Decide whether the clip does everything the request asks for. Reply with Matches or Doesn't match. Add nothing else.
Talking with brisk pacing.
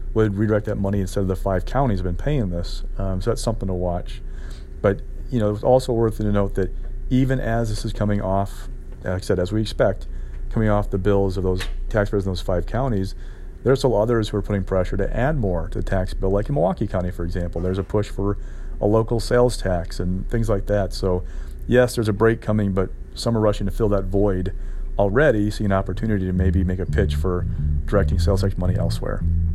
Matches